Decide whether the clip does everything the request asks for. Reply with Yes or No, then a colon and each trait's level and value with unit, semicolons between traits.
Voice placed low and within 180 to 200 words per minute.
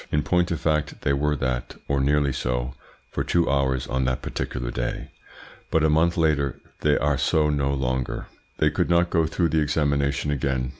Yes: very low, 70 Hz; average, 190 wpm